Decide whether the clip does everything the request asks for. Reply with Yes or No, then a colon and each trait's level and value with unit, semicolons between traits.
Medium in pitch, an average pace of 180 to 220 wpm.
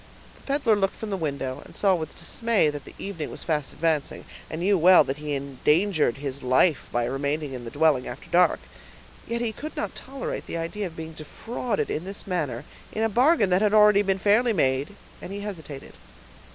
Yes: medium, 170 Hz; average, 200 wpm